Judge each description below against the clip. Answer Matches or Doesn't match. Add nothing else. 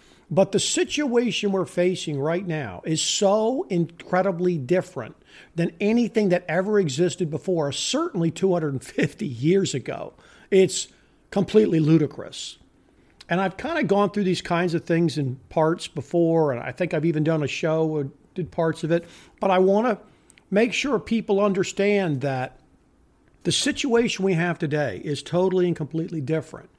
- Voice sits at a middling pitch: Matches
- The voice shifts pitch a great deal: Doesn't match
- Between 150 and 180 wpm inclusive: Matches